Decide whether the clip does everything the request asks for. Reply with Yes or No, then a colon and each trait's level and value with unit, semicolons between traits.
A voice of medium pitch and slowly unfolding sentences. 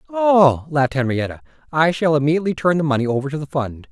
No: medium, 150 Hz; average, 200 wpm